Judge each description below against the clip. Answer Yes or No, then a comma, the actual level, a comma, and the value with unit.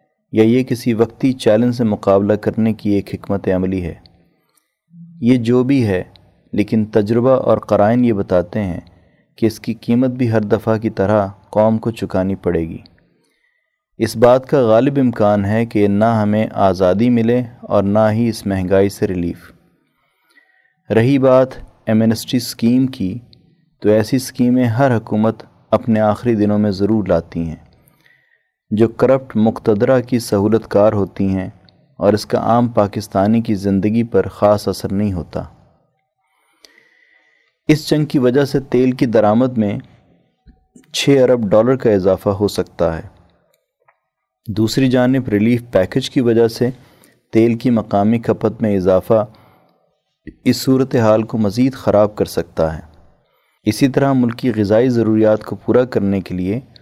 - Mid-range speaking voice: No, low, 110 Hz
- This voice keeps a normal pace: Yes, average, 150 wpm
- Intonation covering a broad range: No, average, 3.6 semitones